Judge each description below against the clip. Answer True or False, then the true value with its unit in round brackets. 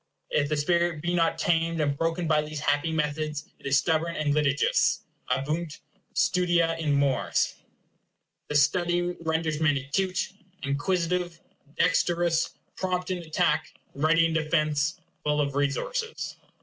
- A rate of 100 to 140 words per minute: True (135 wpm)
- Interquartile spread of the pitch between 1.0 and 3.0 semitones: True (2.6 semitones)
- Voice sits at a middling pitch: True (160 Hz)